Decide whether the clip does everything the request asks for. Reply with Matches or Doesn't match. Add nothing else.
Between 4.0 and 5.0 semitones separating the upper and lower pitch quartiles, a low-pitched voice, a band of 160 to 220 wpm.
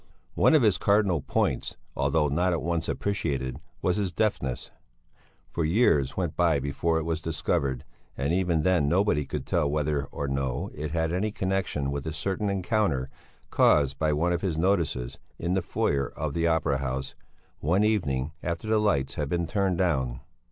Matches